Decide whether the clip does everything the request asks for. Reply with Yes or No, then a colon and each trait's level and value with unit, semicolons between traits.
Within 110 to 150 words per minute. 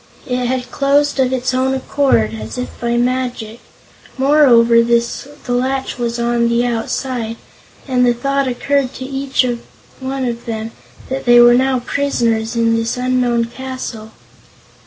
Yes: average, 145 wpm